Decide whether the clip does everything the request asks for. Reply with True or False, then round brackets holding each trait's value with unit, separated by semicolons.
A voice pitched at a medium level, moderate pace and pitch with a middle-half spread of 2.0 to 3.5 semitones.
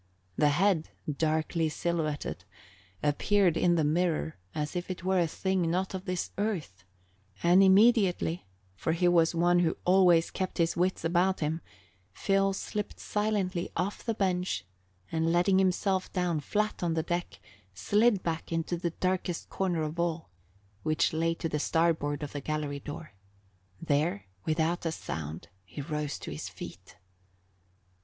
True (170 Hz; 150 wpm; 2.9 semitones)